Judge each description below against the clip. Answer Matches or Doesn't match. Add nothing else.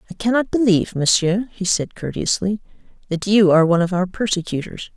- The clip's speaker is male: Doesn't match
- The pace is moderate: Matches